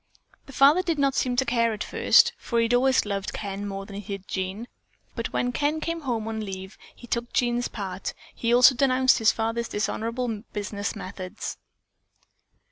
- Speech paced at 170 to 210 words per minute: Yes, average, 190 wpm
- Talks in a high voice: Yes, high, 230 Hz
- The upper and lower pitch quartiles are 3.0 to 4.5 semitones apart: Yes, average, 3.7 semitones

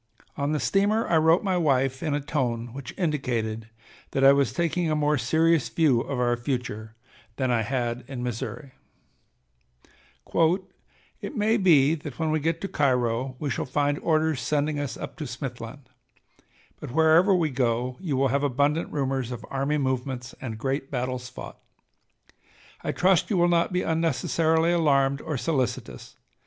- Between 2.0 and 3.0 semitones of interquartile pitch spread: No, average, 4.2 semitones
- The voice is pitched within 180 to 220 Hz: No, medium, 140 Hz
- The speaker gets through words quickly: No, average, 165 wpm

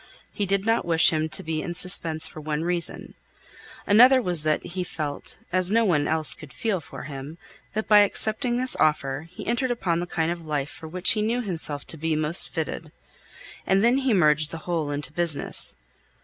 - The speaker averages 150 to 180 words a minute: No, average, 200 wpm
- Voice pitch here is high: No, medium, 170 Hz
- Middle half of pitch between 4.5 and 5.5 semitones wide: Yes, average, 4.8 semitones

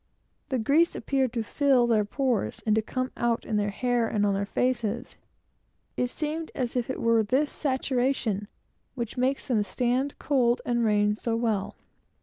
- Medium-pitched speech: No, high, 240 Hz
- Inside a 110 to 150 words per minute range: No, average, 165 wpm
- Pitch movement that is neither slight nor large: Yes, average, 3.2 semitones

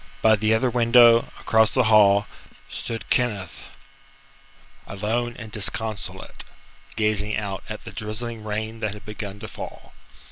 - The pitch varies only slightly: Yes, narrow, 1.6 semitones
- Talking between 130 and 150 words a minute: Yes, slow, 135 wpm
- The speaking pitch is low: Yes, low, 110 Hz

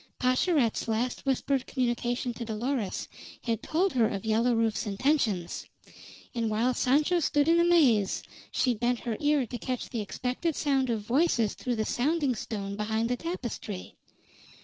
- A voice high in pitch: Yes, high, 245 Hz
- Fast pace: No, average, 150 wpm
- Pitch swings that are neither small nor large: Yes, average, 3.9 semitones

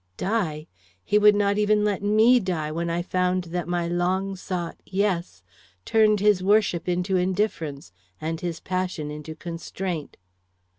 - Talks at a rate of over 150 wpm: No, average, 145 wpm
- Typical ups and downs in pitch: Yes, average, 3.3 semitones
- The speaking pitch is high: No, medium, 180 Hz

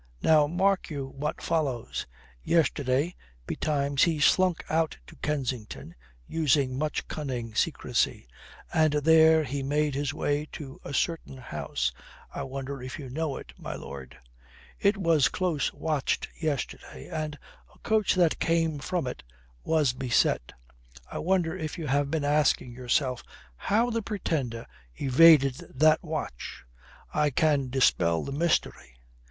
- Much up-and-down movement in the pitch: No, average, 3.4 semitones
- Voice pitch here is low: No, medium, 150 Hz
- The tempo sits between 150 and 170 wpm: No, slow, 135 wpm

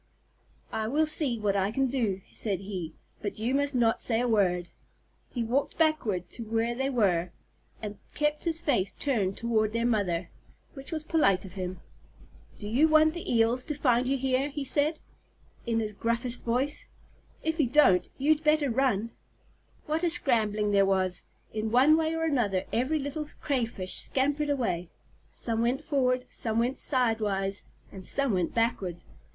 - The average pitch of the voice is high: Yes, high, 235 Hz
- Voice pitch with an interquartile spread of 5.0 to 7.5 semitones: Yes, wide, 5.6 semitones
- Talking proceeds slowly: No, average, 170 wpm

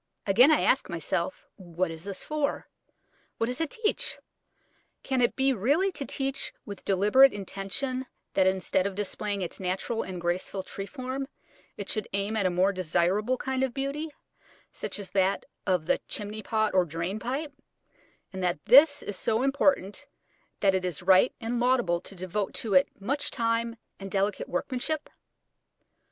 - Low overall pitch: No, high, 205 Hz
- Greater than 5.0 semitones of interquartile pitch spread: Yes, wide, 5.6 semitones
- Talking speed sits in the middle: Yes, average, 165 wpm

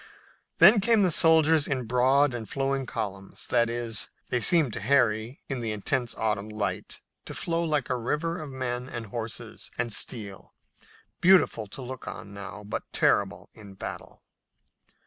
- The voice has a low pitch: Yes, low, 125 Hz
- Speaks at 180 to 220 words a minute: No, average, 160 wpm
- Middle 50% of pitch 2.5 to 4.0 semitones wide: No, average, 4.8 semitones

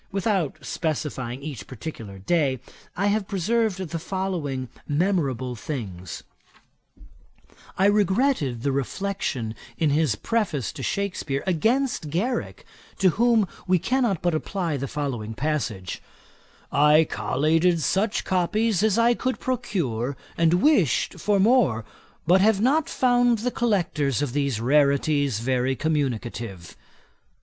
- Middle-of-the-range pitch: Yes, medium, 160 Hz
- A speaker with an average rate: No, slow, 120 wpm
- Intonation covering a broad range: Yes, wide, 7.2 semitones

